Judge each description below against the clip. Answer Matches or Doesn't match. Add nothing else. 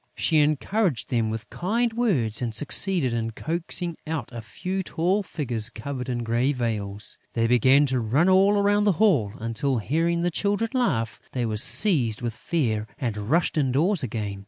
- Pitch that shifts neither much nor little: Doesn't match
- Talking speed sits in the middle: Matches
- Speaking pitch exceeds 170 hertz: Doesn't match